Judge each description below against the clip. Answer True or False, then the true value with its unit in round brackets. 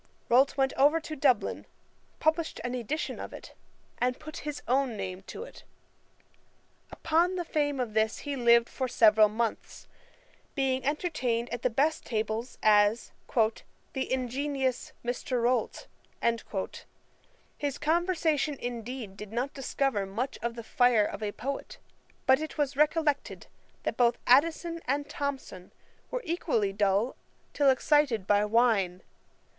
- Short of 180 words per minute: True (135 wpm)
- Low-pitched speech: False (255 Hz)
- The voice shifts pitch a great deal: False (4.4 semitones)